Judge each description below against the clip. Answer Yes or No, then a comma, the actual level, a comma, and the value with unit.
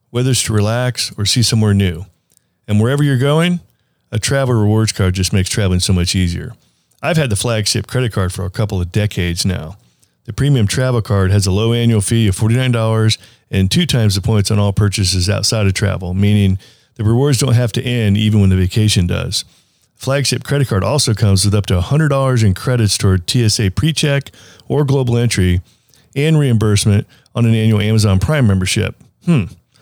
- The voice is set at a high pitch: No, low, 110 Hz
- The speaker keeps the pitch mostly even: No, average, 3.8 semitones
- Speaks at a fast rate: No, average, 190 wpm